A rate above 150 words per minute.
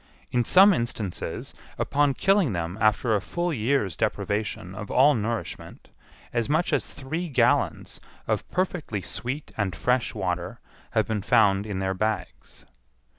No: average, 140 wpm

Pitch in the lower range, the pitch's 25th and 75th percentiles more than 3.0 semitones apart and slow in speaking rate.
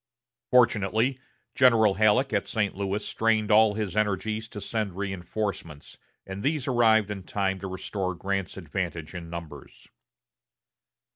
No: low, 100 Hz; narrow, 2.5 semitones; slow, 130 wpm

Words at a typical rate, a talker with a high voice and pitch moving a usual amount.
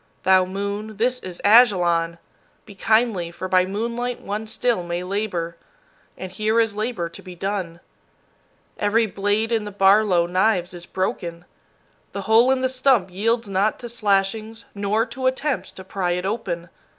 Yes: average, 160 wpm; high, 205 Hz; average, 3.6 semitones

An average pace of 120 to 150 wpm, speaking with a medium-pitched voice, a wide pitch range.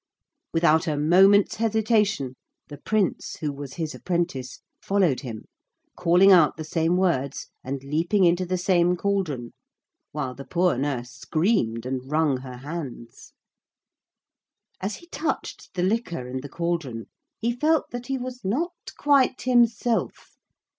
Yes: average, 140 wpm; medium, 170 Hz; wide, 6.8 semitones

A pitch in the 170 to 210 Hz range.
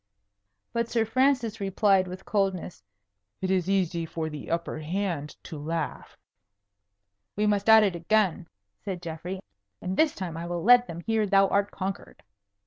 Yes: high, 190 Hz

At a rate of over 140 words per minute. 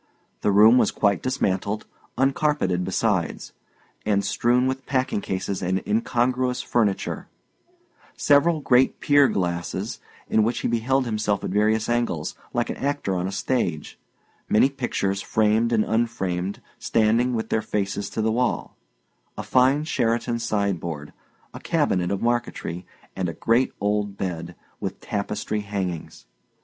No: slow, 135 wpm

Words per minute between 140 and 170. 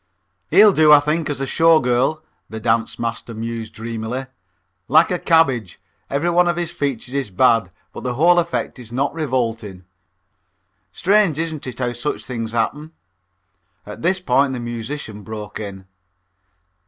Yes: average, 155 wpm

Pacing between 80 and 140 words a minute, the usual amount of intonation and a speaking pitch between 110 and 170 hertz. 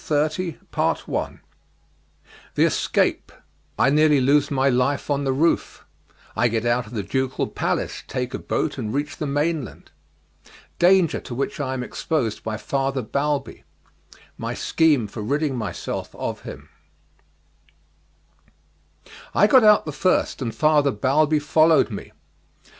Yes: slow, 135 wpm; average, 3.5 semitones; medium, 140 Hz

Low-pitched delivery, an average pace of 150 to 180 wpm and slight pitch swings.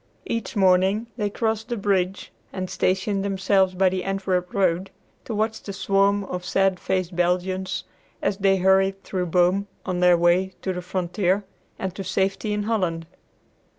No: high, 190 Hz; average, 160 wpm; narrow, 1.5 semitones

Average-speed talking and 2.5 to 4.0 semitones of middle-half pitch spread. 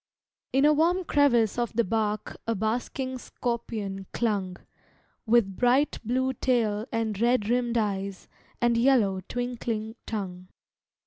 No: slow, 125 wpm; average, 3.0 semitones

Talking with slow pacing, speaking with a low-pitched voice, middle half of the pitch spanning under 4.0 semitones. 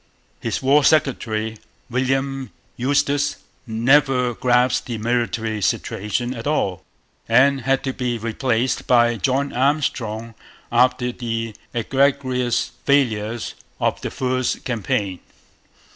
Yes: slow, 105 wpm; low, 125 Hz; average, 2.9 semitones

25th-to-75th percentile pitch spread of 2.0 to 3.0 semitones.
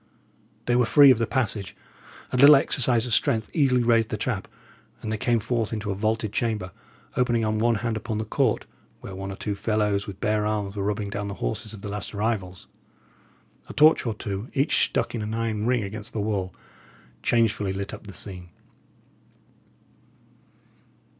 Yes: narrow, 2.5 semitones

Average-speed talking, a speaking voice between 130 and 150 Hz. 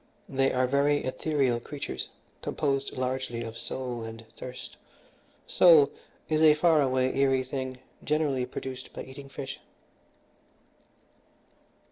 No: slow, 115 wpm; low, 135 Hz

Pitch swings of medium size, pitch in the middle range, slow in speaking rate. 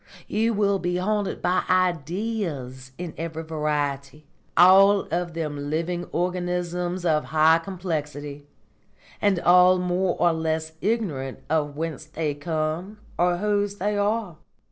Yes: average, 3.3 semitones; medium, 175 Hz; slow, 125 wpm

